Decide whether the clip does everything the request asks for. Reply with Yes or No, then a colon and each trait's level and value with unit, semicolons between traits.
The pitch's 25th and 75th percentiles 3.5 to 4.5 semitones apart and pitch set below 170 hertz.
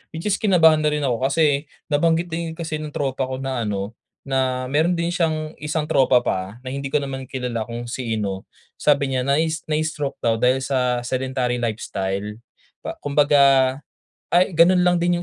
Yes: average, 4.0 semitones; medium, 140 Hz